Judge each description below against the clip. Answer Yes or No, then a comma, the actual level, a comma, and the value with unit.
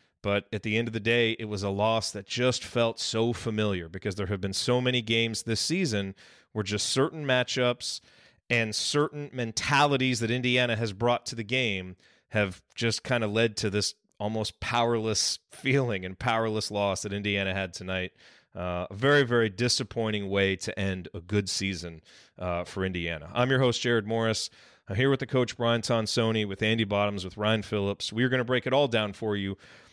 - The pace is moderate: Yes, average, 195 wpm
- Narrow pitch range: No, average, 3.3 semitones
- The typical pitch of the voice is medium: No, low, 110 Hz